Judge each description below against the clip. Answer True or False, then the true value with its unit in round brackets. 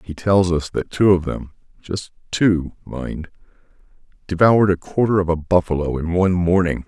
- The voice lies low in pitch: True (90 Hz)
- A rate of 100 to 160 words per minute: True (150 wpm)